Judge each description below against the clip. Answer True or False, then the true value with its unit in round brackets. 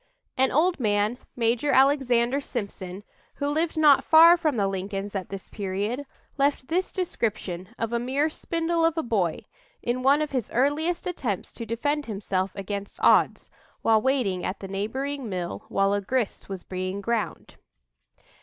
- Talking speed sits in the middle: True (160 wpm)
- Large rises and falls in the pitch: True (6.4 semitones)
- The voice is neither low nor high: False (235 Hz)